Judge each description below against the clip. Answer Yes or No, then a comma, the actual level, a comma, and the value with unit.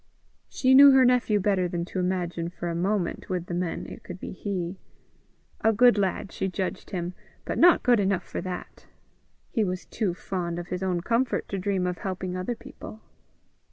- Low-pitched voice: No, medium, 185 Hz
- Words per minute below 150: No, average, 195 wpm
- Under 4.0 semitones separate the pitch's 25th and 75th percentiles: Yes, average, 3.0 semitones